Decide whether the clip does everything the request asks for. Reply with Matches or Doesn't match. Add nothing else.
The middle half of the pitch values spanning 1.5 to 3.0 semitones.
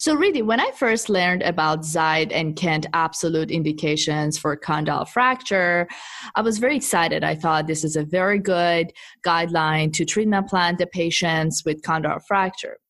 Doesn't match